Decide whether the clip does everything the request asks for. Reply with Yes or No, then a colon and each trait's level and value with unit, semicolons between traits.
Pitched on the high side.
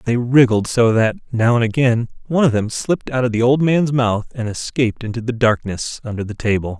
No: low, 120 Hz